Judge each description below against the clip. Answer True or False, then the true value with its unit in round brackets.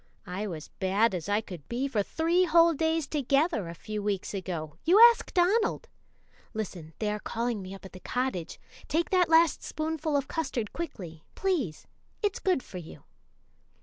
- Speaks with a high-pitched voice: True (235 Hz)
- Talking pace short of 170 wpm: False (175 wpm)